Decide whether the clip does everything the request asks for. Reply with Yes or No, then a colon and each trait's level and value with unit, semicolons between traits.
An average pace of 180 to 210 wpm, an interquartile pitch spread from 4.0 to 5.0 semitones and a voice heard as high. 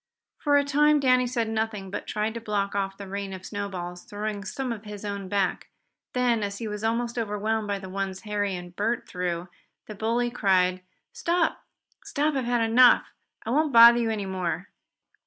No: average, 190 wpm; average, 3.4 semitones; high, 210 Hz